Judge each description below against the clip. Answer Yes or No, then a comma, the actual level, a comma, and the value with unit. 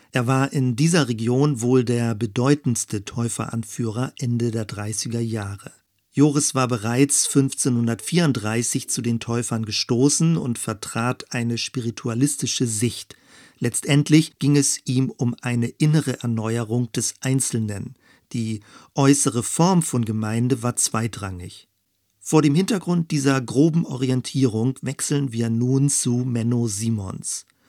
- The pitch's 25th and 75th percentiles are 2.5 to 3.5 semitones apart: Yes, average, 3.2 semitones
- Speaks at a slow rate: Yes, slow, 120 wpm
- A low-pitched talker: Yes, low, 125 Hz